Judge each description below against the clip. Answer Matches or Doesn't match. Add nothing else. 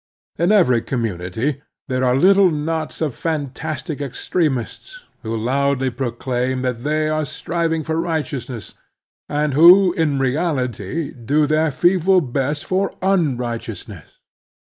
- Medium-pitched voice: Matches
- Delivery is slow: Matches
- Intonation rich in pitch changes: Doesn't match